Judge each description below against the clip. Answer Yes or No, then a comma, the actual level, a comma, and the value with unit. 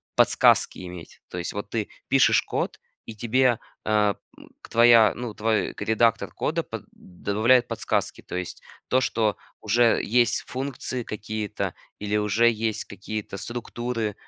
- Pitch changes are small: Yes, narrow, 2.3 semitones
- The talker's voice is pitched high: No, low, 110 Hz